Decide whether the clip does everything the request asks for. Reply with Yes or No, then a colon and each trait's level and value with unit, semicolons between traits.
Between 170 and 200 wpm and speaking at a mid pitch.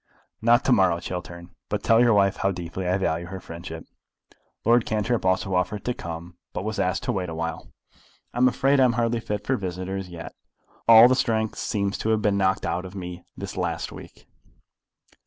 No: average, 195 wpm; very low, 95 Hz